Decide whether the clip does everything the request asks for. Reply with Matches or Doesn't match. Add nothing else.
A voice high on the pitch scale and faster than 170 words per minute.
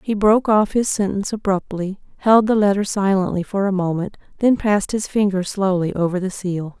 Matches